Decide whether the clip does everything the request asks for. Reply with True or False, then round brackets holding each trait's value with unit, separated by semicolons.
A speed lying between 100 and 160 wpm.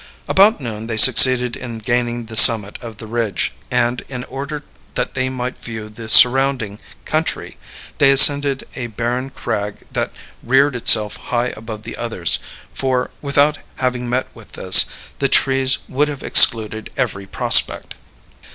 True (150 wpm)